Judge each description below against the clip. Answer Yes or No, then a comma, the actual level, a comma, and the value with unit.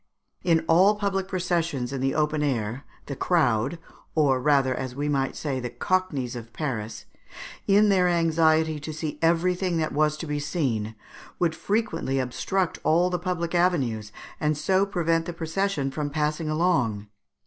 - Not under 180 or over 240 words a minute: No, average, 160 wpm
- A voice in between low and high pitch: Yes, medium, 155 Hz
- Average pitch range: Yes, average, 4.5 semitones